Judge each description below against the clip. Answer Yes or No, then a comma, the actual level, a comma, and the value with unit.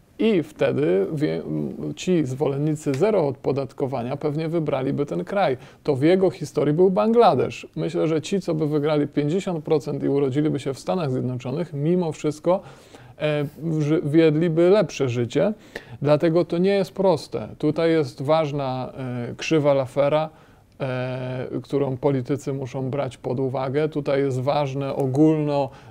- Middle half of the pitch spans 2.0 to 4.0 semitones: Yes, average, 2.9 semitones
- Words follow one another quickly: No, average, 125 wpm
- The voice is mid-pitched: Yes, medium, 145 Hz